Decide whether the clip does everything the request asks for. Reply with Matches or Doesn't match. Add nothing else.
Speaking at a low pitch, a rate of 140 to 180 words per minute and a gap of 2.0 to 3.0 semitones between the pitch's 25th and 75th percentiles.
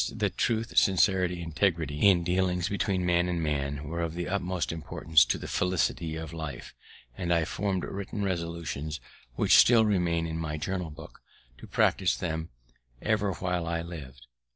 Matches